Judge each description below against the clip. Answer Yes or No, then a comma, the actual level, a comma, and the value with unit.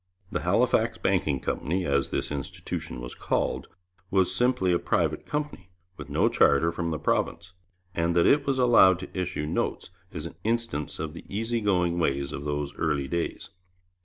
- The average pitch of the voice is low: Yes, very low, 85 Hz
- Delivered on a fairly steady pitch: No, average, 4.8 semitones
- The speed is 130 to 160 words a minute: No, average, 170 wpm